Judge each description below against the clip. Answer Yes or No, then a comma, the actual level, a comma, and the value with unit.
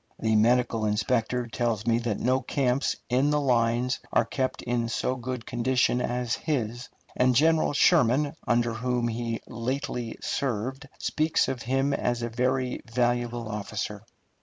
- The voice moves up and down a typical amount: No, narrow, 2.0 semitones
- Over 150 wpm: No, average, 145 wpm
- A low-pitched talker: Yes, low, 120 Hz